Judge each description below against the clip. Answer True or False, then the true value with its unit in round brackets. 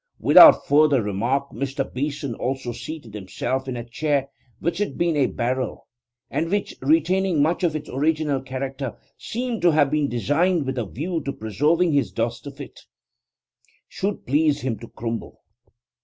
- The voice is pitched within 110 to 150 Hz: True (140 Hz)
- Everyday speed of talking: True (160 wpm)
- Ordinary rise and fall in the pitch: True (3.8 semitones)